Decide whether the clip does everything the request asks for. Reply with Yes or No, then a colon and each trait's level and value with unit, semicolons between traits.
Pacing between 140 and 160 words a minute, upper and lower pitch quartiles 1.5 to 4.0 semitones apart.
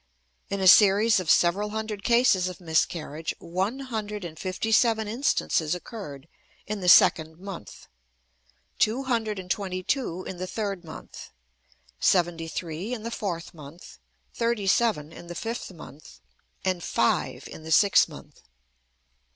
No: average, 145 wpm; average, 4.4 semitones